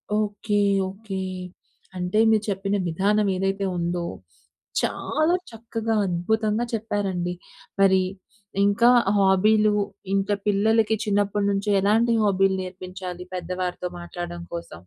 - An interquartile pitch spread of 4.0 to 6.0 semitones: No, narrow, 2.6 semitones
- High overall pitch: Yes, high, 200 Hz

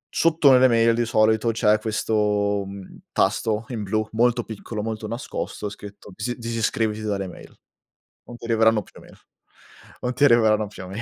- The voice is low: Yes, low, 110 Hz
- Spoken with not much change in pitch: Yes, narrow, 1.9 semitones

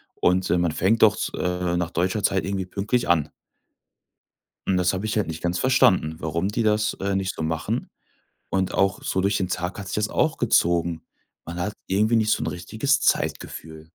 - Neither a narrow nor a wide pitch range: Yes, average, 3.3 semitones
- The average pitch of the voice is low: Yes, very low, 95 Hz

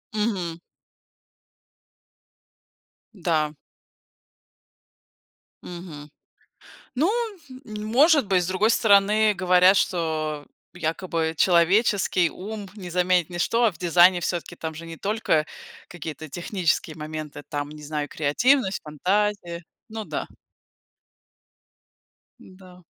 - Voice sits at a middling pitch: Yes, medium, 180 Hz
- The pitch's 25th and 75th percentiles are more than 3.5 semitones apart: Yes, average, 4.1 semitones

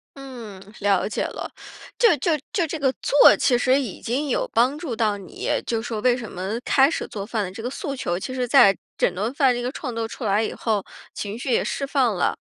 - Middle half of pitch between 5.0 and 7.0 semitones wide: No, average, 4.4 semitones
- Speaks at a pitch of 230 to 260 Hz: Yes, high, 240 Hz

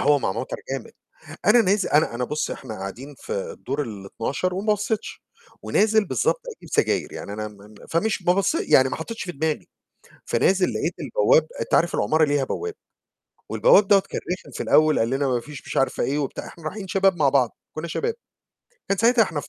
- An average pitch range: No, wide, 7.1 semitones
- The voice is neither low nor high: Yes, medium, 155 Hz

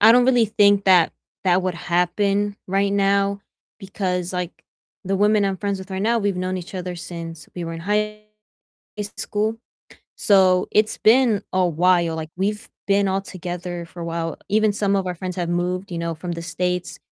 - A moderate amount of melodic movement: No, narrow, 2.3 semitones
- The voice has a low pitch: No, high, 190 Hz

